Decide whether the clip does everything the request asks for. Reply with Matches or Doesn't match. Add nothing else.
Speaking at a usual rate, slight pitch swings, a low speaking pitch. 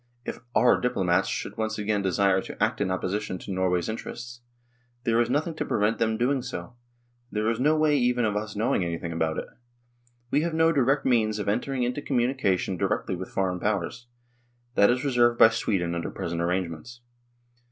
Doesn't match